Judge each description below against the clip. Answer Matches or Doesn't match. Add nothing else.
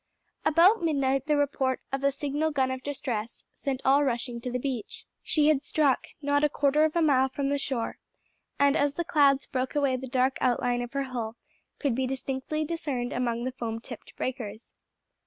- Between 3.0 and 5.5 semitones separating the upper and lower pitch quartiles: Doesn't match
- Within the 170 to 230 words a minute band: Matches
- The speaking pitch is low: Doesn't match